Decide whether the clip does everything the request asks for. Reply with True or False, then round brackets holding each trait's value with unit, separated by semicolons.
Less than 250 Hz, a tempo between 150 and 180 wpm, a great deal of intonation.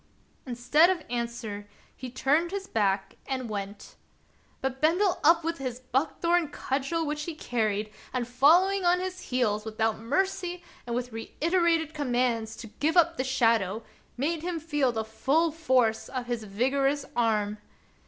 False (260 Hz; 155 wpm; 6.3 semitones)